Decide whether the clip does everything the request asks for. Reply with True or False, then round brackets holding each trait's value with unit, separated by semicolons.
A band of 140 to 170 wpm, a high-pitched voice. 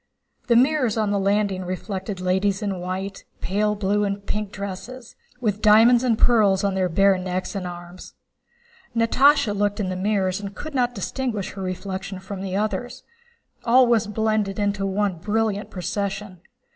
True (160 wpm; 200 Hz)